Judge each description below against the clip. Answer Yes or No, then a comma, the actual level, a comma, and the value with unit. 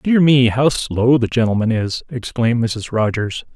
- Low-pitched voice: Yes, low, 120 Hz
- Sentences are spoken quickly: No, average, 150 wpm